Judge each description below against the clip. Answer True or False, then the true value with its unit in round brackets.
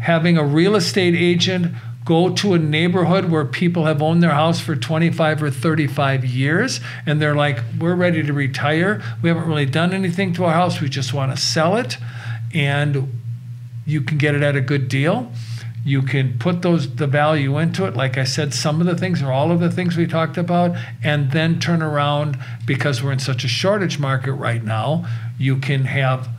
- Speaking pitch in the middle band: True (150 Hz)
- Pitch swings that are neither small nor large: True (4.1 semitones)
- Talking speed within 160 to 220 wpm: True (200 wpm)